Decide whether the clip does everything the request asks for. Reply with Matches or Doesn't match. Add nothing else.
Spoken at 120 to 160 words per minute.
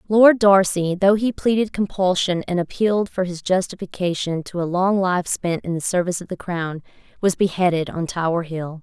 Doesn't match